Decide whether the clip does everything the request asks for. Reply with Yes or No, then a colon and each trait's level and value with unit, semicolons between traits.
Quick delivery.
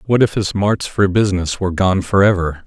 Yes: fast, 225 wpm